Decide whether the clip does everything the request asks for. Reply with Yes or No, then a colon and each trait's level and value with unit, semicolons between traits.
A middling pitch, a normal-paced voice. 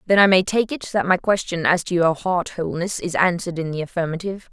No: medium, 175 Hz; fast, 240 wpm